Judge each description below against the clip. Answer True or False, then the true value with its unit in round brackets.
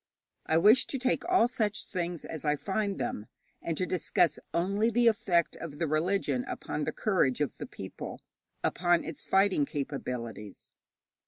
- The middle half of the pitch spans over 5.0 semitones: True (5.5 semitones)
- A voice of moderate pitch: True (175 Hz)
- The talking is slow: False (160 wpm)